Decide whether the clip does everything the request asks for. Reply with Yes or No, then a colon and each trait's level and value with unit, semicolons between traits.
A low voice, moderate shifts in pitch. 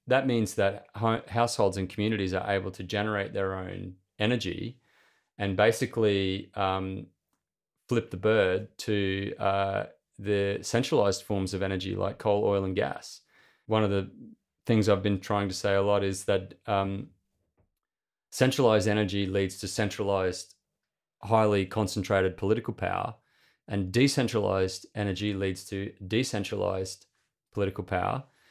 No: low, 100 Hz; narrow, 2.1 semitones